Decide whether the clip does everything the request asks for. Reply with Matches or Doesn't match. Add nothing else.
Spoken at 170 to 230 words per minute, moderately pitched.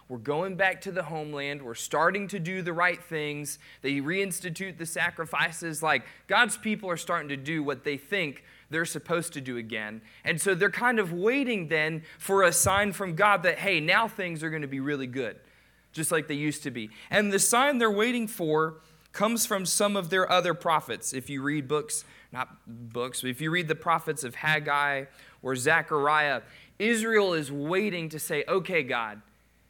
Matches